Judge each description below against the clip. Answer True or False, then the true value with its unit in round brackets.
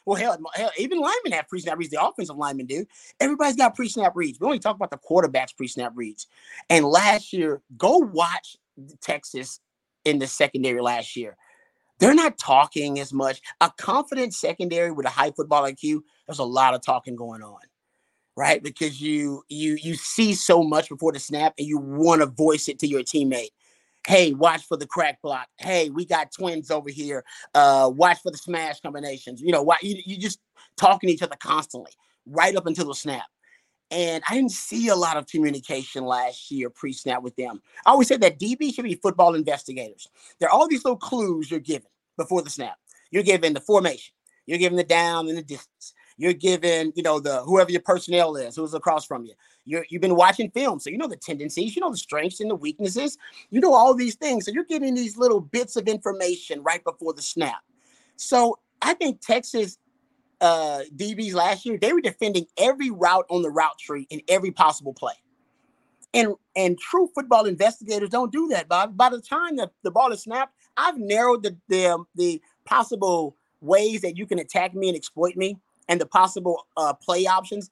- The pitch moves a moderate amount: False (6.7 semitones)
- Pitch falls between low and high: True (175 Hz)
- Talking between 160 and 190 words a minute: False (200 wpm)